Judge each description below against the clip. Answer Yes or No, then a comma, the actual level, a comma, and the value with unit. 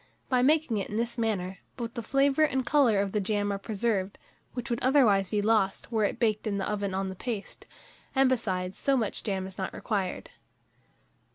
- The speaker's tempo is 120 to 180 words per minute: No, average, 200 wpm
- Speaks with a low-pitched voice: No, high, 215 Hz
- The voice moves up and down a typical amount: Yes, average, 3.9 semitones